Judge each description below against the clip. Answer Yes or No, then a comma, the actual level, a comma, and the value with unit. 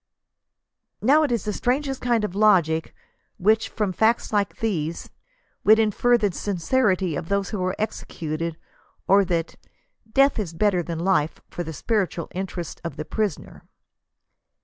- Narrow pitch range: No, average, 4.5 semitones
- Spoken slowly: No, average, 150 wpm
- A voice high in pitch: Yes, high, 200 Hz